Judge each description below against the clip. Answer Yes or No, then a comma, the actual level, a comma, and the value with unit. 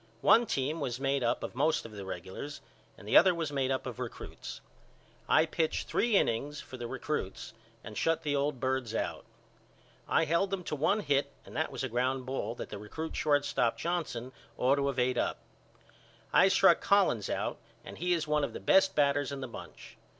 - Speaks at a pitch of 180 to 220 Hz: No, medium, 140 Hz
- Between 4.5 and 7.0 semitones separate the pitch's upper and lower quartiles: No, average, 3.8 semitones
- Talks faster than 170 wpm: Yes, average, 200 wpm